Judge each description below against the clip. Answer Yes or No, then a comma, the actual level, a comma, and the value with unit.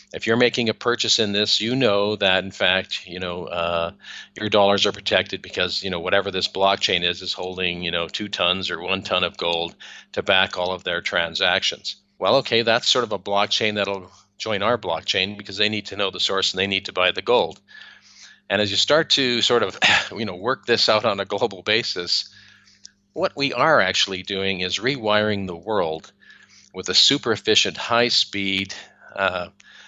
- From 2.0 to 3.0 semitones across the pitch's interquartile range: Yes, average, 2.7 semitones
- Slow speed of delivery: No, average, 200 wpm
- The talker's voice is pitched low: Yes, low, 100 Hz